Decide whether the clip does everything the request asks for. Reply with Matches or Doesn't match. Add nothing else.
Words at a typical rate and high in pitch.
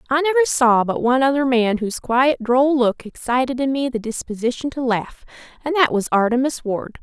Matches